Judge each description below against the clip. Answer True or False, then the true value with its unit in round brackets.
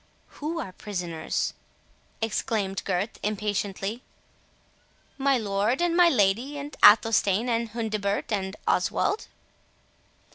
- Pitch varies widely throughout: False (4.2 semitones)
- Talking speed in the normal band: False (100 wpm)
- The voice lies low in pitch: False (215 Hz)